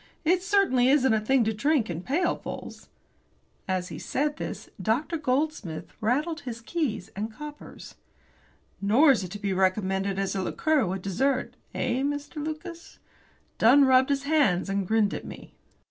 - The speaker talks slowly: No, average, 160 wpm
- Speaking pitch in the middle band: No, very high, 250 Hz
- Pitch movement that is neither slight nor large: No, wide, 7.0 semitones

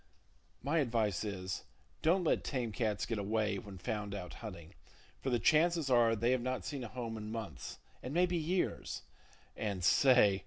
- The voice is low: Yes, low, 115 Hz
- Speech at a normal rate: Yes, average, 165 wpm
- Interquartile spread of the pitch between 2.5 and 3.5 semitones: No, average, 4.4 semitones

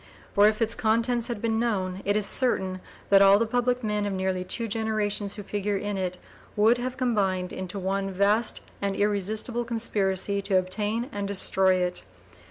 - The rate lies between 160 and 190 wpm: Yes, average, 180 wpm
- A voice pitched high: Yes, high, 205 Hz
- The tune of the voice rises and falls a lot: No, average, 2.8 semitones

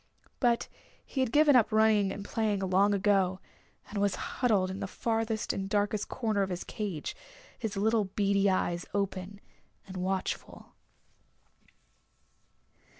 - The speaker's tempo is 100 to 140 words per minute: Yes, slow, 135 wpm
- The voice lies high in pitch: Yes, high, 200 Hz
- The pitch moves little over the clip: Yes, narrow, 2.3 semitones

